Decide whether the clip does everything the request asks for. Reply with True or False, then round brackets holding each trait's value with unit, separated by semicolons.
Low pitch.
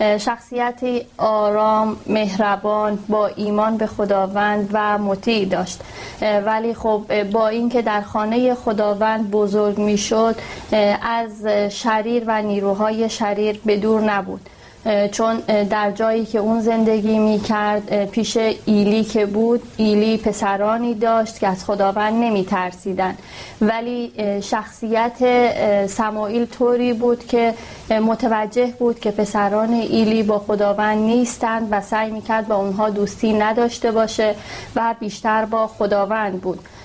False (215 Hz)